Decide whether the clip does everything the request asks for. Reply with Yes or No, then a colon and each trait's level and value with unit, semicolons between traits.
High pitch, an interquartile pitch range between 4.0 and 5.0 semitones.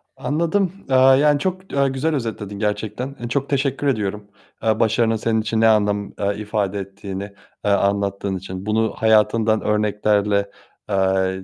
No: low, 110 Hz; average, 4.4 semitones